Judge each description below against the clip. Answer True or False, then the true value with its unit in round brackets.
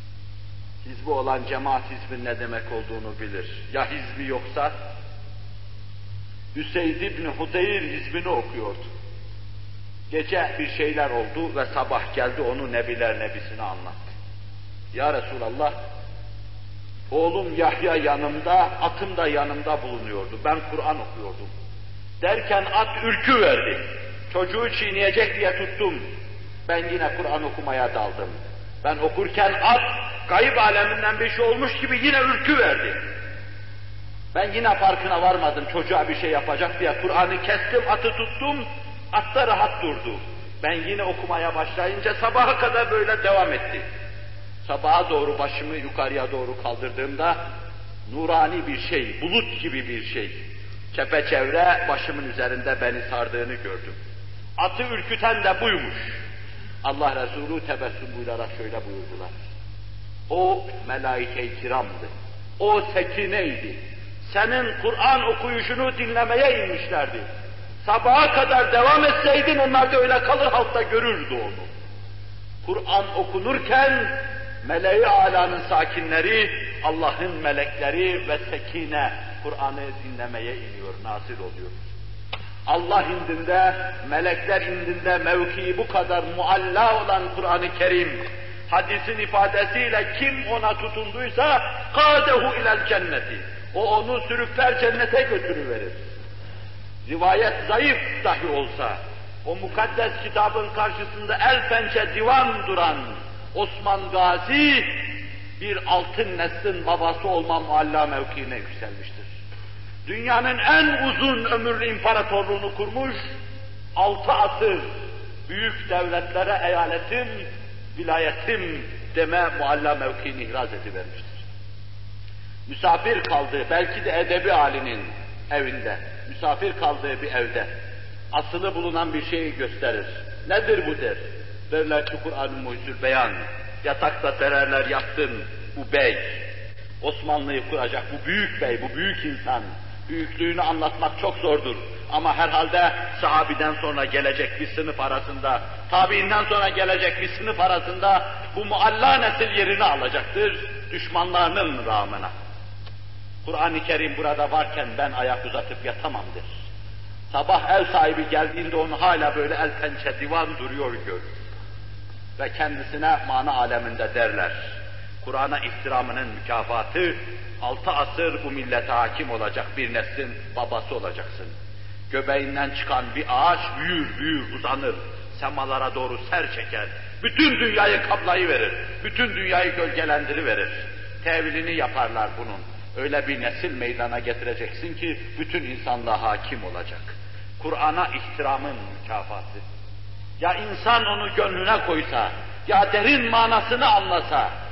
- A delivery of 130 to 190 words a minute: False (110 wpm)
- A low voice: True (125 Hz)